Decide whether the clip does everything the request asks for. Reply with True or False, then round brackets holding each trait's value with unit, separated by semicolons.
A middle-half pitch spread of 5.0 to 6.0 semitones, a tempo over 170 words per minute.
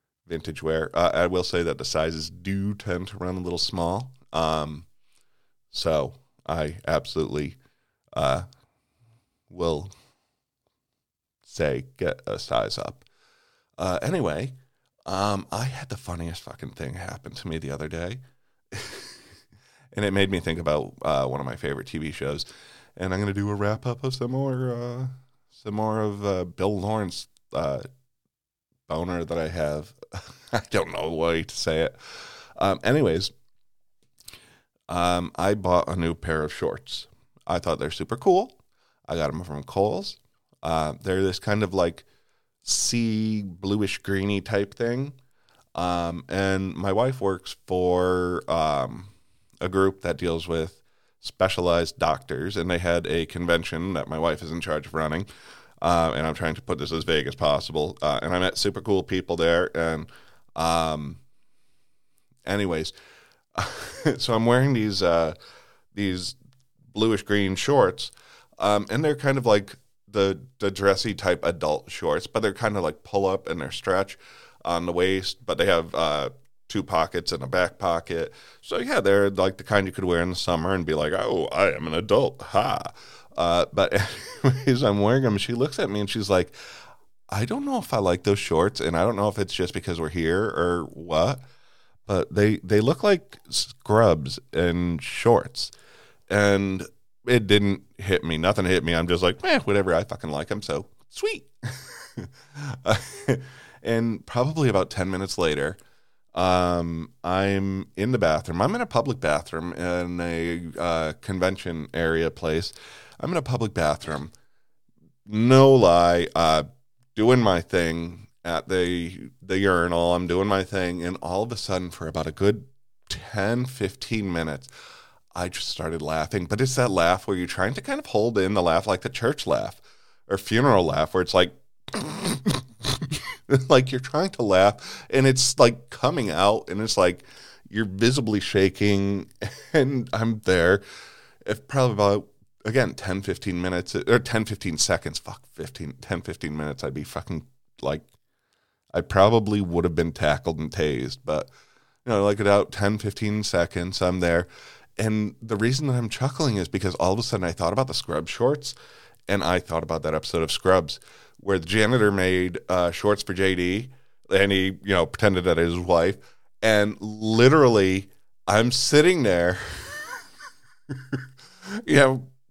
False (5.3 semitones; 165 wpm)